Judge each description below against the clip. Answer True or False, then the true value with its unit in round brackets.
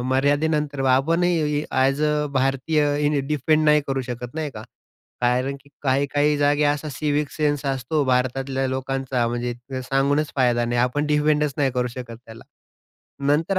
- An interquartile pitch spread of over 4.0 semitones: False (2.4 semitones)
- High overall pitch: False (140 Hz)